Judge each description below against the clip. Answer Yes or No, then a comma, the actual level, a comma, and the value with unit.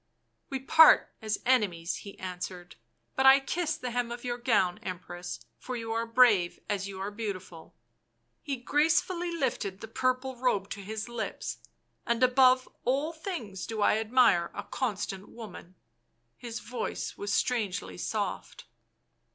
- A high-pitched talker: Yes, high, 230 Hz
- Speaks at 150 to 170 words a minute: Yes, average, 160 wpm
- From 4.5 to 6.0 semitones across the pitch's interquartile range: Yes, average, 4.8 semitones